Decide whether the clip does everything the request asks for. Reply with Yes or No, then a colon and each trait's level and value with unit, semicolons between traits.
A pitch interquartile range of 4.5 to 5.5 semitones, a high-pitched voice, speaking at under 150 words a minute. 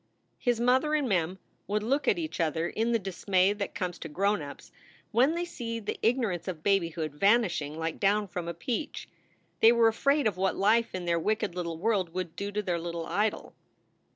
No: average, 5.1 semitones; high, 200 Hz; fast, 205 wpm